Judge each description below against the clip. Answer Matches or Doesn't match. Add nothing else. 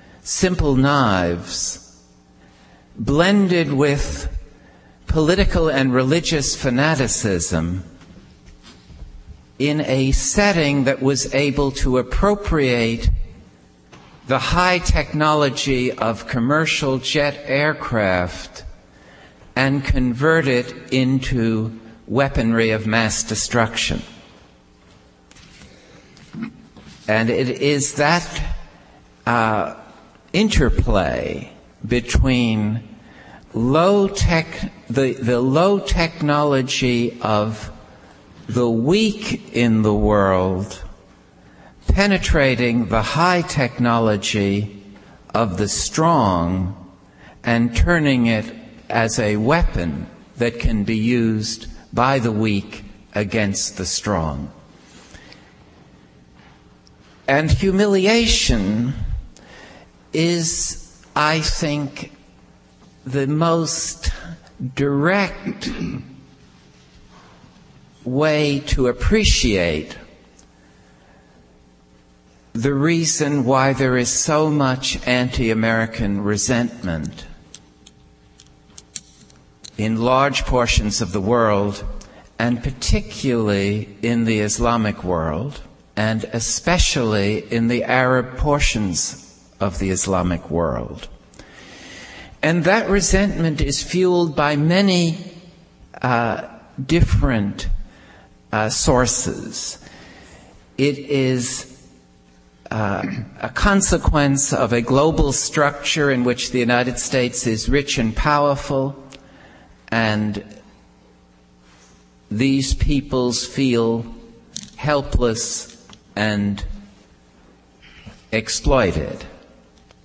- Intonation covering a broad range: Matches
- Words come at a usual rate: Doesn't match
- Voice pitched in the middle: Doesn't match